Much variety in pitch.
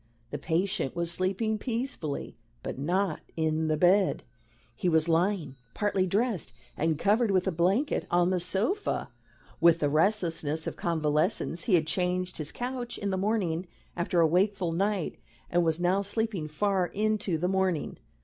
No: average, 3.8 semitones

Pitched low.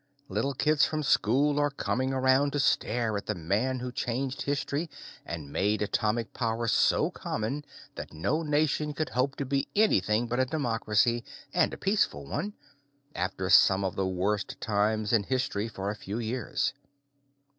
Yes: low, 120 Hz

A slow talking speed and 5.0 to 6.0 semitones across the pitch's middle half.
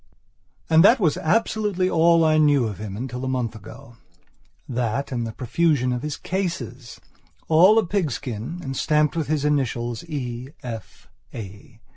No: average, 155 wpm; wide, 5.4 semitones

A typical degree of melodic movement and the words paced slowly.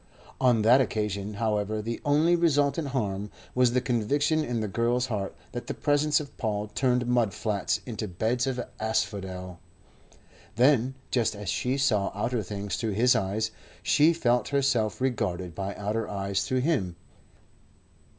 No: average, 4.1 semitones; average, 150 wpm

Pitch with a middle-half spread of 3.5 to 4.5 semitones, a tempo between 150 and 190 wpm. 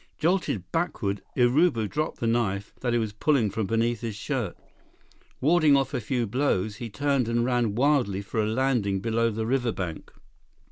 Yes: average, 4.2 semitones; average, 170 wpm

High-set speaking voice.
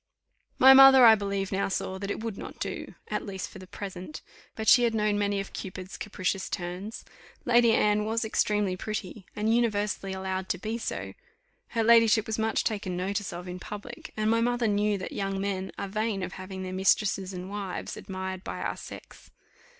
Yes: high, 205 Hz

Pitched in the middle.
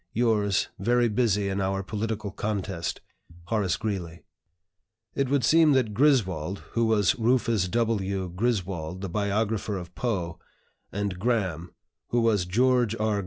No: low, 105 Hz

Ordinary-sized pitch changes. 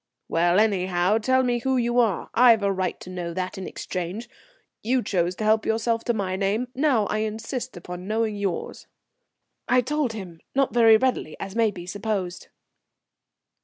Yes: average, 4.3 semitones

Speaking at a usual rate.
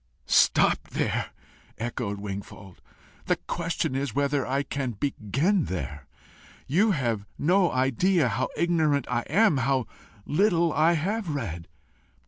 No: slow, 120 wpm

